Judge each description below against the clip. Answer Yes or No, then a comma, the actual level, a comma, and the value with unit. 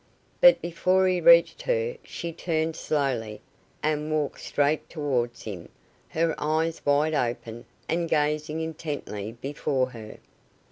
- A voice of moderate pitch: Yes, medium, 155 Hz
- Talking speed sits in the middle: No, slow, 125 wpm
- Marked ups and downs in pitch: No, average, 3.7 semitones